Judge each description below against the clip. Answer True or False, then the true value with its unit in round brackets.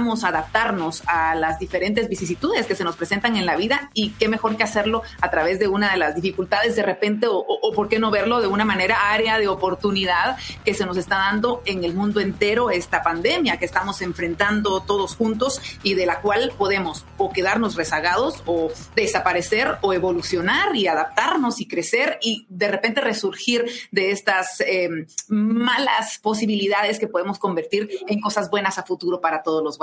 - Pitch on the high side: True (200 Hz)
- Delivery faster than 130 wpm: True (185 wpm)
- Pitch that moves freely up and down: False (3.3 semitones)